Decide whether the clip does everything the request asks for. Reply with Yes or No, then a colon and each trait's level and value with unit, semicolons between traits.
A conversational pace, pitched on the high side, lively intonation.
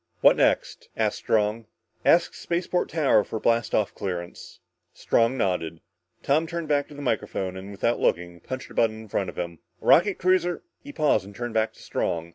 No: average, 195 wpm; low, 115 Hz; wide, 7.8 semitones